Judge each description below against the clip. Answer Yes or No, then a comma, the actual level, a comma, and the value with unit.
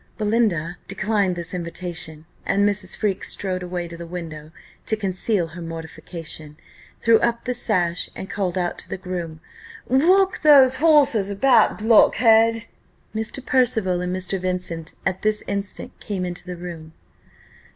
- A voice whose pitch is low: No, medium, 185 Hz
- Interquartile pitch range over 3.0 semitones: Yes, average, 4.3 semitones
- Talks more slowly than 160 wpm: Yes, average, 145 wpm